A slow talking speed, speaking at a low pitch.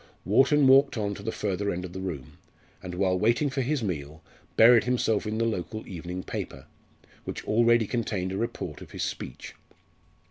No: average, 180 wpm; low, 105 Hz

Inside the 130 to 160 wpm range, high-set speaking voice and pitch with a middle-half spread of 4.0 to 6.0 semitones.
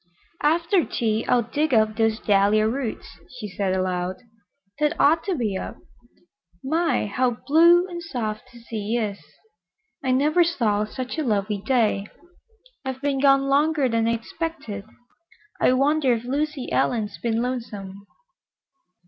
Yes: average, 140 wpm; high, 245 Hz; wide, 5.4 semitones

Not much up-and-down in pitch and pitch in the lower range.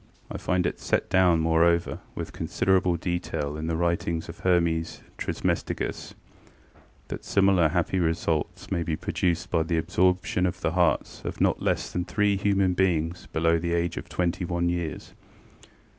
Yes: narrow, 1.7 semitones; very low, 85 Hz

